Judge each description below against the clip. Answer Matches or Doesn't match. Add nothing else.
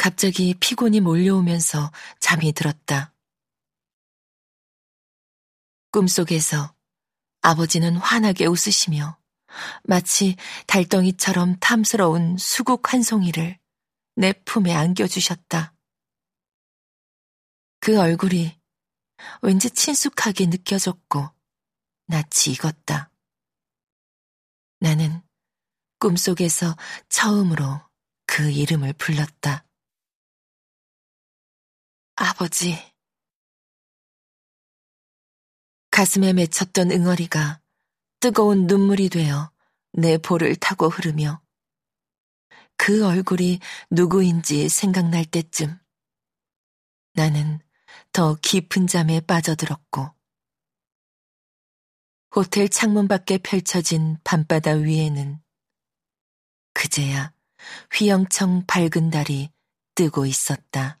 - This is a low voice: Doesn't match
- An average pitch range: Matches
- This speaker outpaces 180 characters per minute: Doesn't match